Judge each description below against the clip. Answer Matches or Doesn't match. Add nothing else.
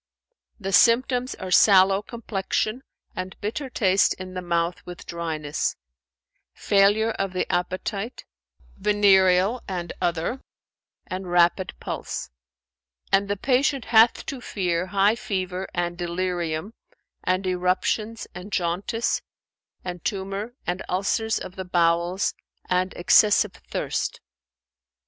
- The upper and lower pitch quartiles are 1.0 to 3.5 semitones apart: Matches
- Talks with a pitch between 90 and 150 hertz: Doesn't match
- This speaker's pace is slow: Matches